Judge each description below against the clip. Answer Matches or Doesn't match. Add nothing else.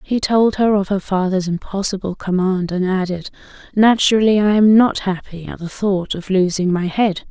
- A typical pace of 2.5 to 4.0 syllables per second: Doesn't match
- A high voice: Matches